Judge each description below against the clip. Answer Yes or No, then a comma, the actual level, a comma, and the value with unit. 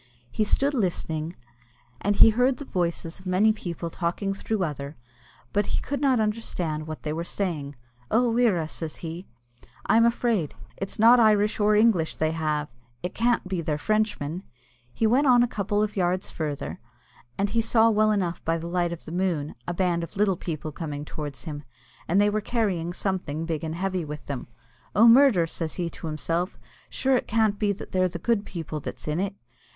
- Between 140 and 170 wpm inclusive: No, average, 195 wpm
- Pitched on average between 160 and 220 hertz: Yes, medium, 185 Hz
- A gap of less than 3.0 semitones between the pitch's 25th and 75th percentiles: No, average, 4.8 semitones